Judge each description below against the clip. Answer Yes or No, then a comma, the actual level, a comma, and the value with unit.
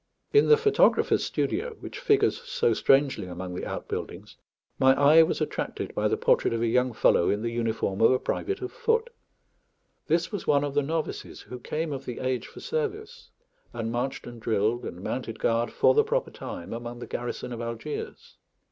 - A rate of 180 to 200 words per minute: Yes, average, 190 wpm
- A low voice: Yes, low, 130 Hz